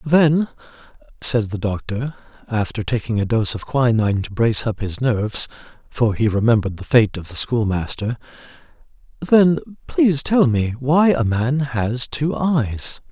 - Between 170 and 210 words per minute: No, average, 150 wpm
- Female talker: No, male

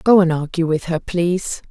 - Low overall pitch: No, medium, 170 Hz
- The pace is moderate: No, fast, 210 wpm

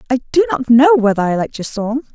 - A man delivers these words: No, female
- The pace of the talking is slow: No, fast, 250 wpm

